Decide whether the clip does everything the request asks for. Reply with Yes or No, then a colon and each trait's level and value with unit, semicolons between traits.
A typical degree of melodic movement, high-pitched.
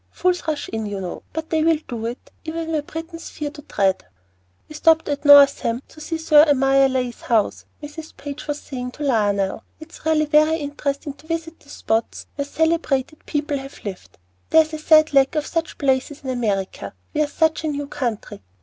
Yes: average, 3.4 semitones; very high, 290 Hz